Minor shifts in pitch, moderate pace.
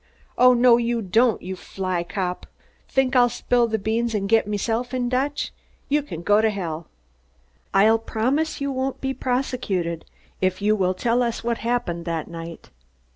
No: average, 4.8 semitones; average, 170 wpm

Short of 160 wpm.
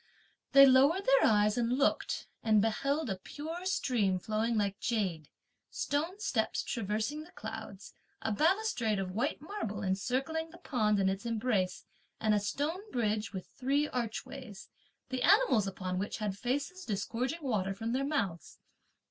Yes: average, 150 wpm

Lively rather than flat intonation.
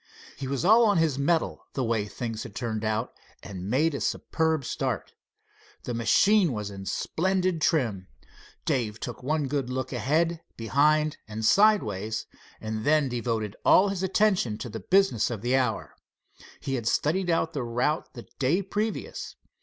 Yes: wide, 6.5 semitones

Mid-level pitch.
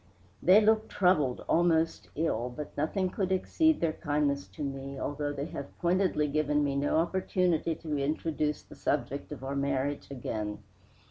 Yes: medium, 150 Hz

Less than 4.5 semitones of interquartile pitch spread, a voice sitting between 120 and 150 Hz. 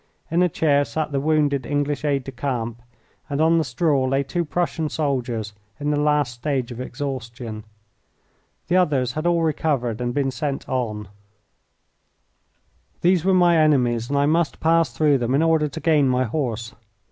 Yes: average, 4.0 semitones; medium, 140 Hz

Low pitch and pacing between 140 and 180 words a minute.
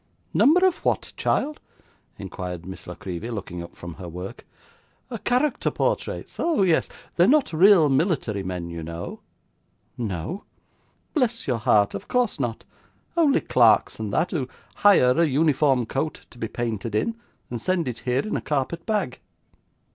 Yes: low, 130 Hz; average, 155 wpm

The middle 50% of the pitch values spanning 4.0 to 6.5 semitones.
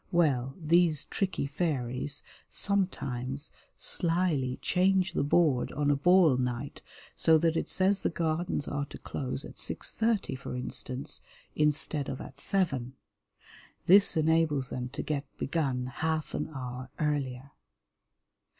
Yes: average, 4.4 semitones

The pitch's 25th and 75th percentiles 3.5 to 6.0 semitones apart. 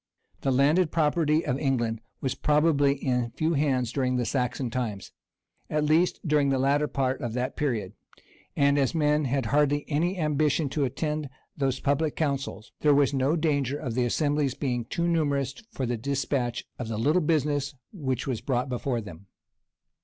No: average, 2.9 semitones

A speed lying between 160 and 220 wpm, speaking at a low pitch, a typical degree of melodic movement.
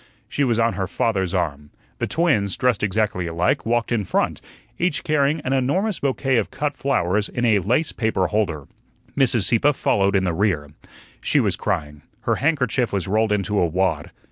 No: average, 180 wpm; low, 110 Hz; wide, 5.8 semitones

